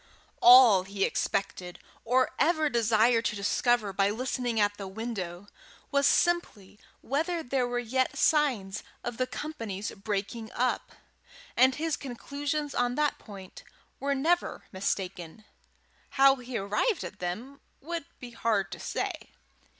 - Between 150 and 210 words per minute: No, slow, 135 wpm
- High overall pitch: Yes, high, 240 Hz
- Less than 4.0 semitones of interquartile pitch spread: No, average, 5.3 semitones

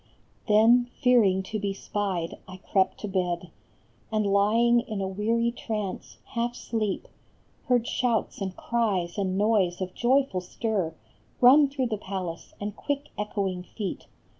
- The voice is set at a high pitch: Yes, high, 210 Hz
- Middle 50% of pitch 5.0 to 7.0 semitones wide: No, average, 3.8 semitones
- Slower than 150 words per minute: Yes, average, 140 wpm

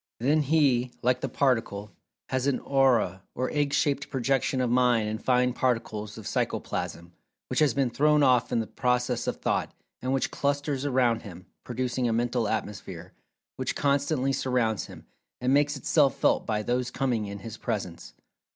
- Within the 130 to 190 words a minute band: Yes, average, 170 wpm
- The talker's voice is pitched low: Yes, low, 125 Hz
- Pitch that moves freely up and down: No, average, 3.3 semitones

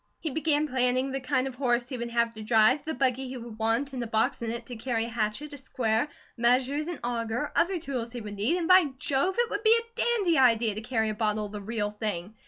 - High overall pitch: Yes, high, 245 Hz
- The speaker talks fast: Yes, fast, 255 wpm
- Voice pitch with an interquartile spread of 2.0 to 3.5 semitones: No, average, 4.1 semitones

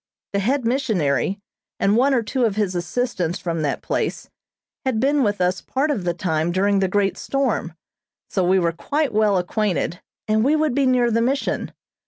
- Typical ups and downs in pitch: No, wide, 6.1 semitones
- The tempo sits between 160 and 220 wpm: Yes, average, 190 wpm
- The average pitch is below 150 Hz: No, high, 210 Hz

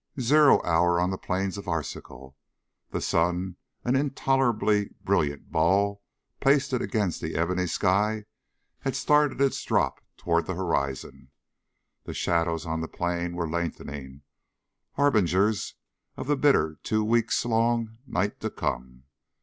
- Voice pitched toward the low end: Yes, very low, 95 Hz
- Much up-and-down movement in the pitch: Yes, wide, 5.8 semitones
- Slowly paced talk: Yes, slow, 130 wpm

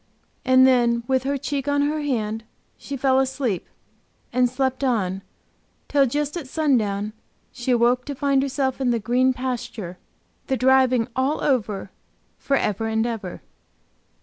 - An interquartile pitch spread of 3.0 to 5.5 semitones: No, narrow, 2.6 semitones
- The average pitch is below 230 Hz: No, very high, 255 Hz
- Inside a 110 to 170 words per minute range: Yes, average, 150 wpm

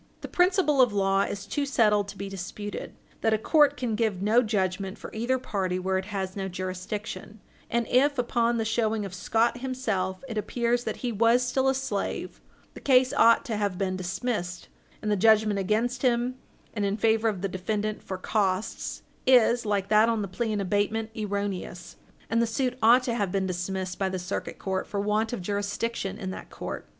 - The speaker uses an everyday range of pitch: Yes, average, 3.4 semitones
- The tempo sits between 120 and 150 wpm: No, average, 200 wpm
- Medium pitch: No, high, 215 Hz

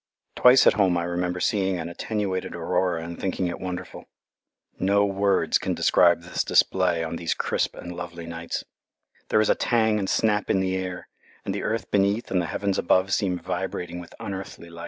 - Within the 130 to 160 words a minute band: No, average, 190 wpm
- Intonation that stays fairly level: Yes, narrow, 2.3 semitones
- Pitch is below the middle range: Yes, very low, 95 Hz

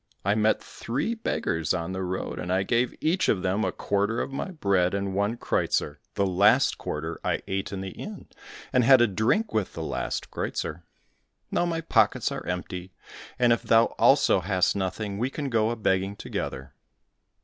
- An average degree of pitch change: Yes, average, 4.1 semitones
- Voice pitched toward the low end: Yes, low, 100 Hz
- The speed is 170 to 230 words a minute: Yes, average, 185 wpm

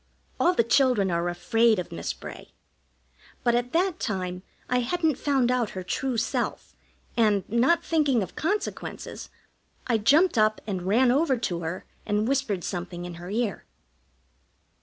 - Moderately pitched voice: No, high, 230 Hz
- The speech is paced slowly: No, average, 155 wpm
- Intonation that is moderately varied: No, wide, 6.3 semitones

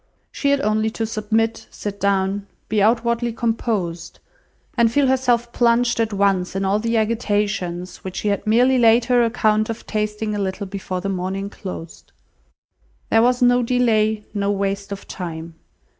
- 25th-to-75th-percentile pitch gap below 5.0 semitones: Yes, average, 2.9 semitones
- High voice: Yes, high, 215 Hz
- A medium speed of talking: Yes, average, 160 wpm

